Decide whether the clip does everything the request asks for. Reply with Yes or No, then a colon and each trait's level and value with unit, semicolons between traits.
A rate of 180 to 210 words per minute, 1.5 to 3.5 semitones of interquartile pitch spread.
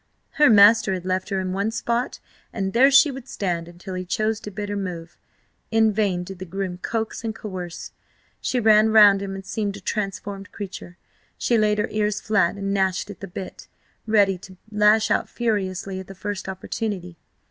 Yes: average, 190 wpm; narrow, 2.5 semitones